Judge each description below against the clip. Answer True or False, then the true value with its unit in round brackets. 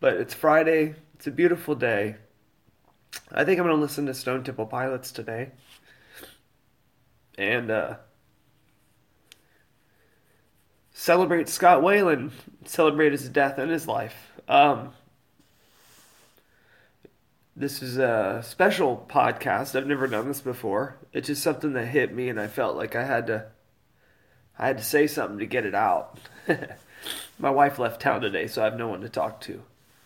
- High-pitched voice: False (135 Hz)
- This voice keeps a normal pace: True (150 wpm)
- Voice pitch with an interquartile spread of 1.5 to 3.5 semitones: False (4.4 semitones)